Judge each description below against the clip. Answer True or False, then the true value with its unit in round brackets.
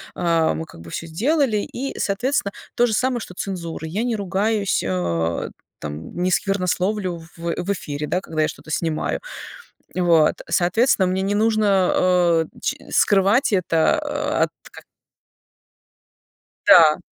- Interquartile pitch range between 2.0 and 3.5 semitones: False (4.3 semitones)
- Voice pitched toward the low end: False (185 Hz)